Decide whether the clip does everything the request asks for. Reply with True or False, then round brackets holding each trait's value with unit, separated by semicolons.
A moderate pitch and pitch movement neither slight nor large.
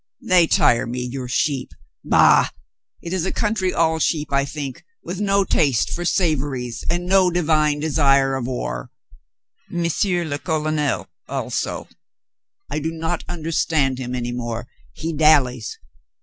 True (150 Hz; 4.3 semitones)